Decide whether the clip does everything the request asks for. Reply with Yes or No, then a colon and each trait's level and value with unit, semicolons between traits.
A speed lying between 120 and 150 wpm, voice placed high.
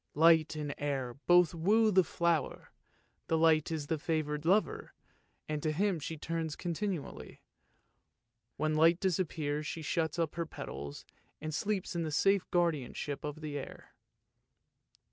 No: average, 145 wpm; medium, 160 Hz